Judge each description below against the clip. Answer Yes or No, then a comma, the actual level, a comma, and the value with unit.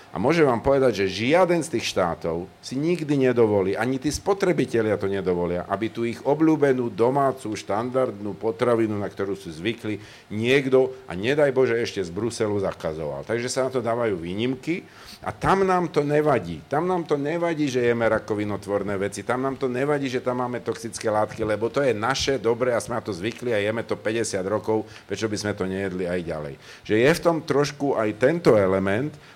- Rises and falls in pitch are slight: No, average, 5.0 semitones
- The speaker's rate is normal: No, fast, 190 wpm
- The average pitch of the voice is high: No, low, 115 Hz